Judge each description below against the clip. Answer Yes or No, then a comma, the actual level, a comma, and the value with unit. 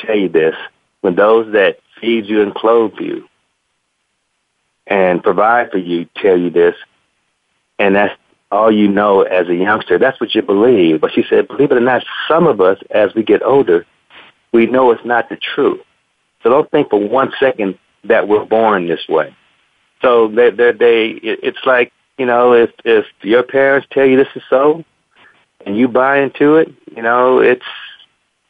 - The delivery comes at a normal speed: Yes, average, 180 wpm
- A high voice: No, low, 130 Hz